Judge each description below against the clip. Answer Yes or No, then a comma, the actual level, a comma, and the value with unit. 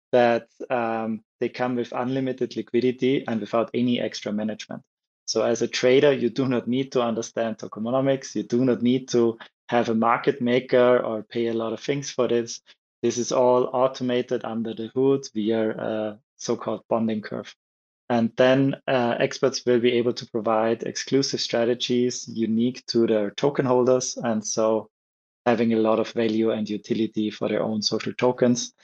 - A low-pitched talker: Yes, low, 120 Hz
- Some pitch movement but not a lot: No, narrow, 1.9 semitones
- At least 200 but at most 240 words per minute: No, average, 175 wpm